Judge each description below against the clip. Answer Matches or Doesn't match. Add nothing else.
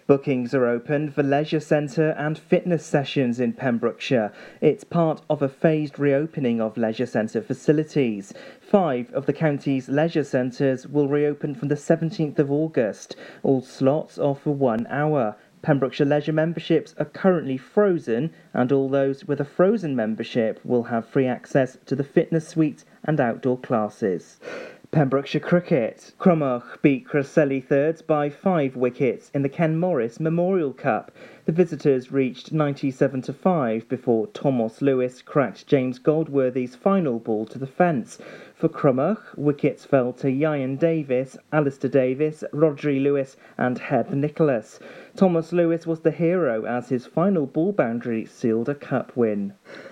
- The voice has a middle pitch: Matches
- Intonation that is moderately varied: Matches